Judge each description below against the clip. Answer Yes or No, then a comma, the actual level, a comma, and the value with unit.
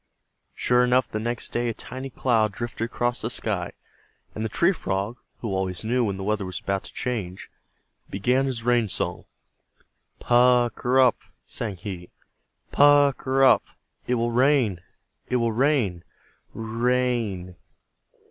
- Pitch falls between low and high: No, low, 120 Hz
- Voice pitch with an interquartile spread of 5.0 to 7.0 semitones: No, average, 3.5 semitones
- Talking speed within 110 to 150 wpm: No, average, 160 wpm